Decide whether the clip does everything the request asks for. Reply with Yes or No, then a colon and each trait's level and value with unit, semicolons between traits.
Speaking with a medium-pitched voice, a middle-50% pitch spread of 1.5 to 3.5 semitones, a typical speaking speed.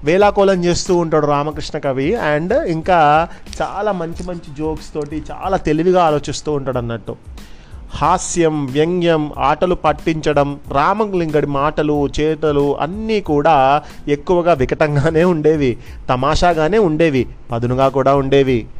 Yes: medium, 155 Hz; average, 3.2 semitones; average, 110 wpm